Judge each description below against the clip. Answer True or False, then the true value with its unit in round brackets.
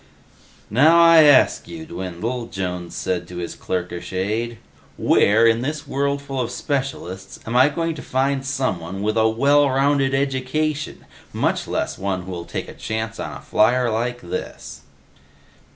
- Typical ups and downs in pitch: False (6.4 semitones)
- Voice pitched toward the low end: True (125 Hz)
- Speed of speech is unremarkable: True (150 wpm)